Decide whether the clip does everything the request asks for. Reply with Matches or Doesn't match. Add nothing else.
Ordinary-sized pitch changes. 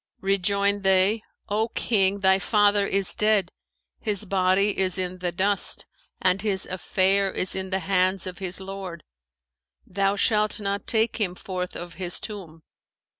Doesn't match